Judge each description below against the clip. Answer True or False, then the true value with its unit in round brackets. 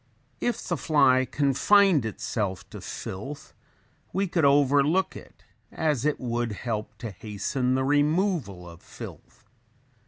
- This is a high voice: False (135 Hz)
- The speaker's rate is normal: False (125 wpm)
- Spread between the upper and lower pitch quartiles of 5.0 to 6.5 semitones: True (5.4 semitones)